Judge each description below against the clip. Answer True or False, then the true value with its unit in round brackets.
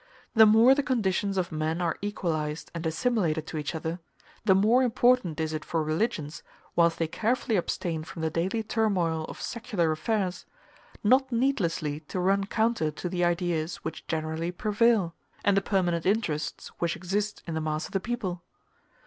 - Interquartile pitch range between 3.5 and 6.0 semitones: True (5.2 semitones)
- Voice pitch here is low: False (180 Hz)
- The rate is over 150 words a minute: True (170 wpm)